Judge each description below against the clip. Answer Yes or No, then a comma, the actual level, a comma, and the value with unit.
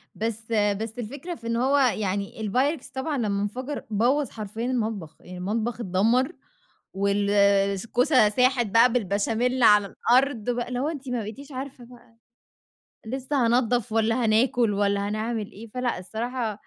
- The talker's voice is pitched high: Yes, high, 230 Hz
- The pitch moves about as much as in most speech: Yes, average, 3.5 semitones